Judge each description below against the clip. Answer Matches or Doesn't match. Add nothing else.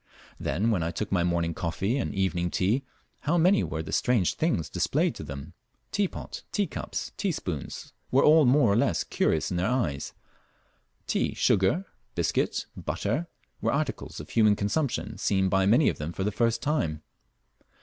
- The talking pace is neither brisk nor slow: Matches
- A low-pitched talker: Matches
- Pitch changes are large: Matches